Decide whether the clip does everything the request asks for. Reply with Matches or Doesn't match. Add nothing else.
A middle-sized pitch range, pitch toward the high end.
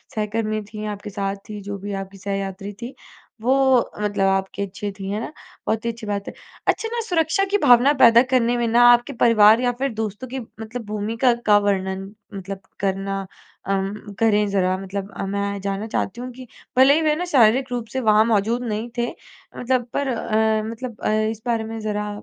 Matches